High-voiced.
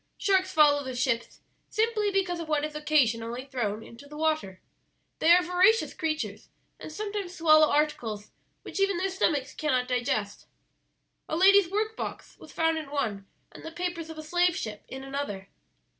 Yes: very high, 310 Hz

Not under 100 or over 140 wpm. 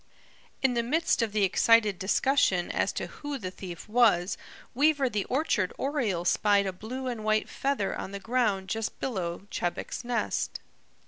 No: average, 165 wpm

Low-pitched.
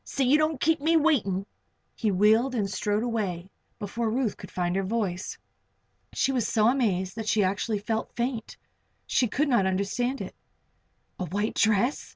No: high, 220 Hz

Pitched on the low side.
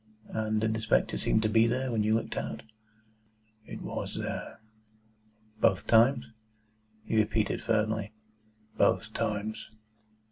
Yes: low, 110 Hz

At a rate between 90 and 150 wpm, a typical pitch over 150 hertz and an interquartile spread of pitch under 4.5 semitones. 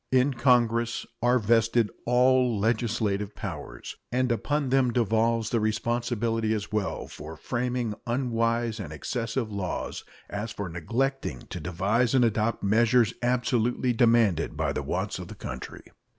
No: slow, 135 wpm; low, 115 Hz; narrow, 2.4 semitones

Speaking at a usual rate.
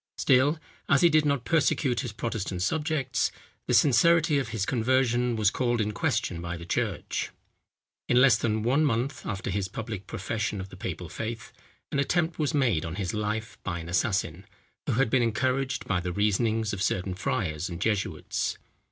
Yes: average, 180 wpm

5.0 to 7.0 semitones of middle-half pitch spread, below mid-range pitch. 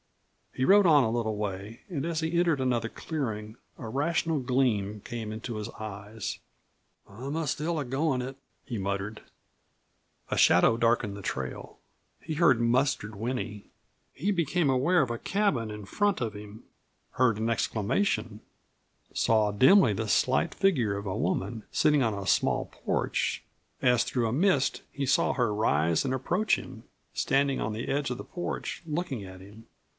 Yes: wide, 5.4 semitones; low, 120 Hz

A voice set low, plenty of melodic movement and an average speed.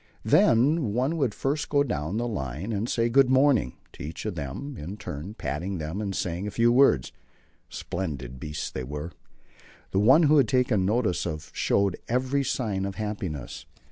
Yes: low, 105 Hz; wide, 8.1 semitones; average, 175 wpm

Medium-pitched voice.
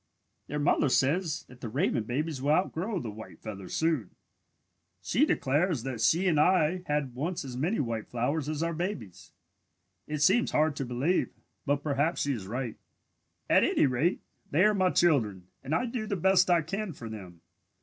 Yes: medium, 150 Hz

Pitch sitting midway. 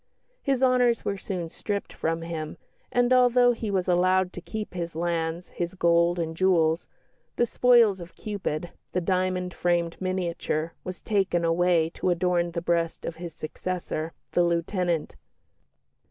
Yes: medium, 175 Hz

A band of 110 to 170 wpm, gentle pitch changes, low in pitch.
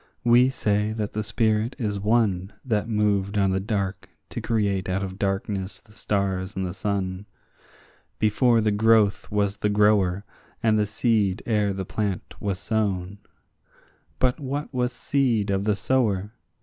Yes: average, 150 wpm; narrow, 2.1 semitones; low, 105 Hz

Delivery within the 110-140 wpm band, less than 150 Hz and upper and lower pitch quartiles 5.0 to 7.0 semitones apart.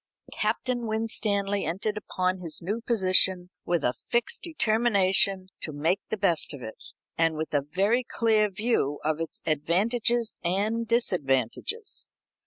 No: slow, 135 wpm; high, 195 Hz; average, 5.3 semitones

